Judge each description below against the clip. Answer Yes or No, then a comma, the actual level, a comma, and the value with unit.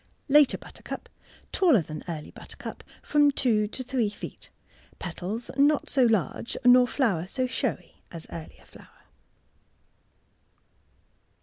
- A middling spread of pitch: No, wide, 7.2 semitones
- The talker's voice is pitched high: Yes, high, 235 Hz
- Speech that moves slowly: Yes, slow, 120 wpm